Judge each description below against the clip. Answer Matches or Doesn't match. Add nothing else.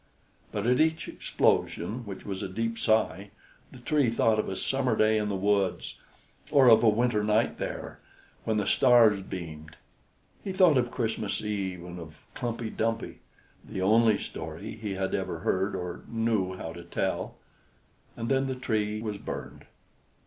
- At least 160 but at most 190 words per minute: Matches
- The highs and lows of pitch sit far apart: Doesn't match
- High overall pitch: Doesn't match